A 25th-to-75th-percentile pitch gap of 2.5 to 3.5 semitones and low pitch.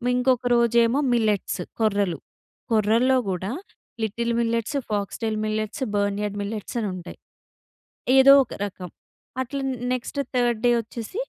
No: average, 2.9 semitones; high, 225 Hz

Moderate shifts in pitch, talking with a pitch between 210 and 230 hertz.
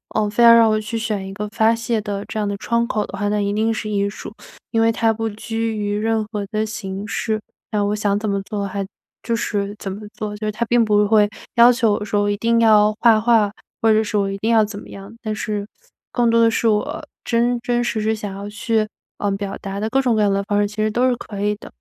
No: narrow, 1.8 semitones; high, 215 Hz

